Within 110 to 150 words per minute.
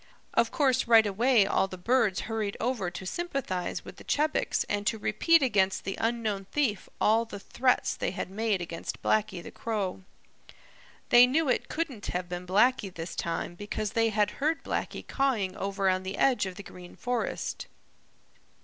No: average, 175 wpm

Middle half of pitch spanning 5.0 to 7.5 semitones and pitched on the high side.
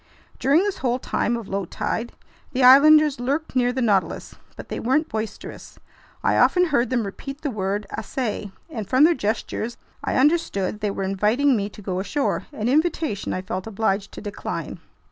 Yes: wide, 5.6 semitones; high, 240 Hz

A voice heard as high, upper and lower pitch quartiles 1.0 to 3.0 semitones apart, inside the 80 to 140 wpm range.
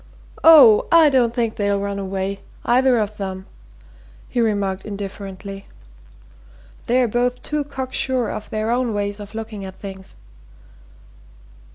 No: high, 215 Hz; average, 3.8 semitones; slow, 135 wpm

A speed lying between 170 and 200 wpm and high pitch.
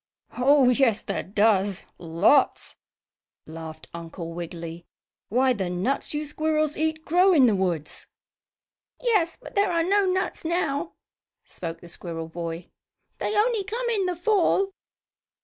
No: slow, 135 wpm; very high, 265 Hz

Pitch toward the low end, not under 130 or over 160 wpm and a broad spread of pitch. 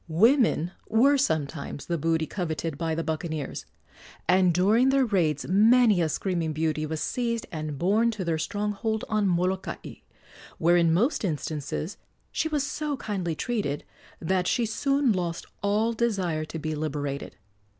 No: medium, 180 Hz; average, 150 wpm; wide, 5.8 semitones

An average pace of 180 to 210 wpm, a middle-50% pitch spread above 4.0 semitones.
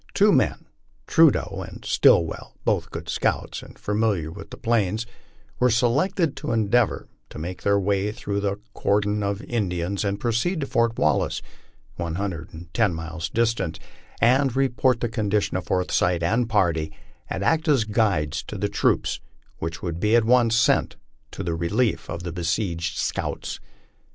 No: average, 165 wpm; average, 5.2 semitones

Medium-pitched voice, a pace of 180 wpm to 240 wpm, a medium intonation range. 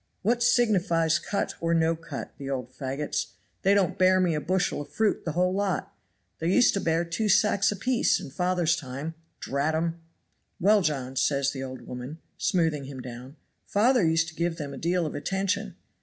Yes: medium, 165 Hz; average, 185 wpm; average, 4.8 semitones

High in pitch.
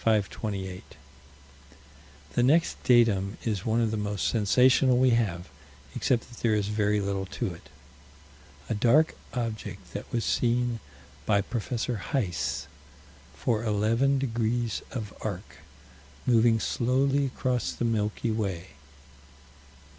No: low, 115 Hz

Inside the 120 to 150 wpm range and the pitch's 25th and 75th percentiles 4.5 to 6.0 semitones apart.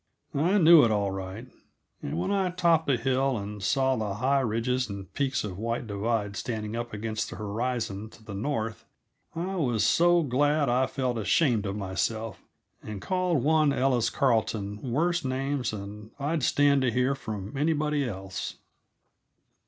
No: average, 160 wpm; average, 5.1 semitones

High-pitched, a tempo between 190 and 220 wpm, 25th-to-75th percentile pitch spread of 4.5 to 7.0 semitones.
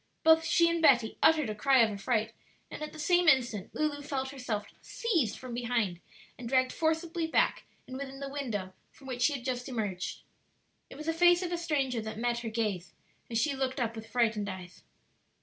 Yes: very high, 255 Hz; average, 200 wpm; average, 5.3 semitones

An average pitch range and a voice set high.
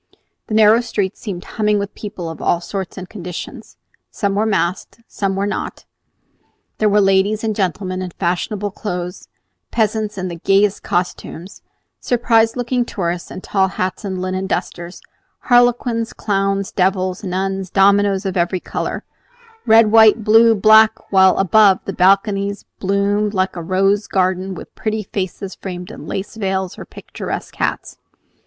No: narrow, 2.3 semitones; high, 195 Hz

